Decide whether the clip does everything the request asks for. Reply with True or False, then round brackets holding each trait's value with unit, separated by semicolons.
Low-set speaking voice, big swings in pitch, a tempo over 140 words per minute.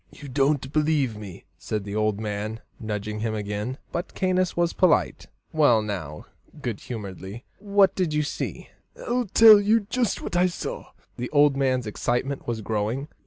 True (130 Hz; 7.9 semitones; 165 wpm)